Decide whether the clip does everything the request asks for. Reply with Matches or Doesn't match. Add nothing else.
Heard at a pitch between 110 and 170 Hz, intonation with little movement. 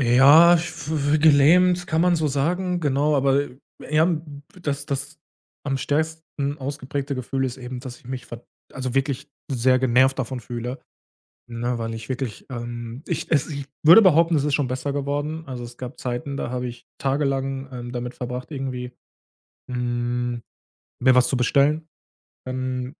Doesn't match